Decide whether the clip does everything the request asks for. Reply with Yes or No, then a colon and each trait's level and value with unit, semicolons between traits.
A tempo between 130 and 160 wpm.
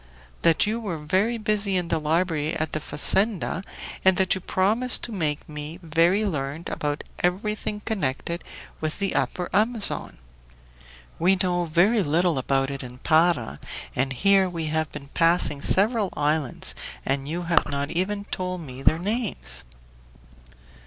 Yes: average, 150 wpm